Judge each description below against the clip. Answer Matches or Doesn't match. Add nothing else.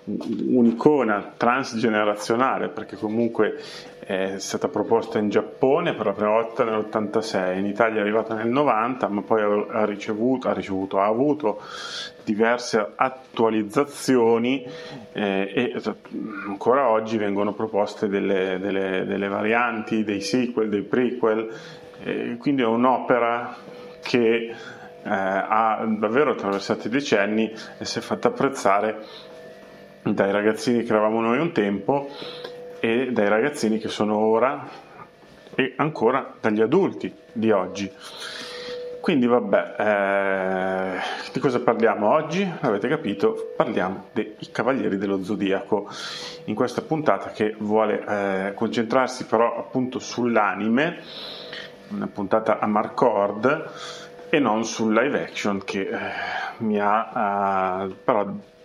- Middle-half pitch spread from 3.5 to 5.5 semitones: Doesn't match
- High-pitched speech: Doesn't match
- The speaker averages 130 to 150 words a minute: Doesn't match